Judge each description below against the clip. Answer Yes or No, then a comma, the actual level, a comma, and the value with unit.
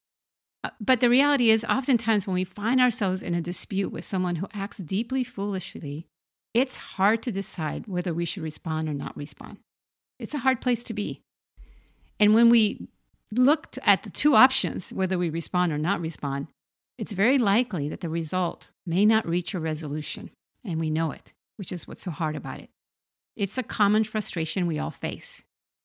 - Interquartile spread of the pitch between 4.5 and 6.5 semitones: Yes, average, 5.2 semitones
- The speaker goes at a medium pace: Yes, average, 180 wpm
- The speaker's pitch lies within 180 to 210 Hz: Yes, high, 190 Hz